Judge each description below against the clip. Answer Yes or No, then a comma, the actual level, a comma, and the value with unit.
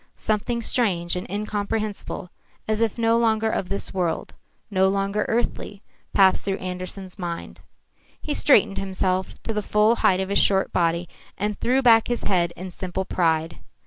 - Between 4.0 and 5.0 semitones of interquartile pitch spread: No, average, 3.0 semitones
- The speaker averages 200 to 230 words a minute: No, average, 160 wpm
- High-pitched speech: Yes, high, 195 Hz